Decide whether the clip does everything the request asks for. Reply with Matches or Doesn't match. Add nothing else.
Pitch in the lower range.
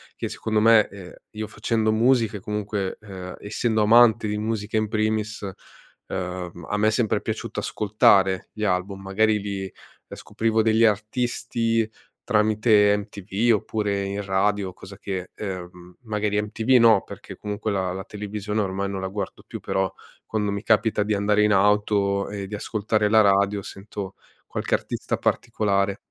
Matches